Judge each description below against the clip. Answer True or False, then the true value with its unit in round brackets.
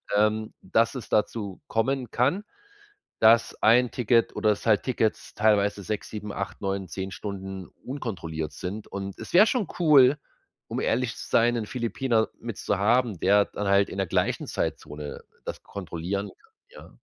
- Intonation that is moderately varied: True (3.4 semitones)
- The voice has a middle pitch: False (105 Hz)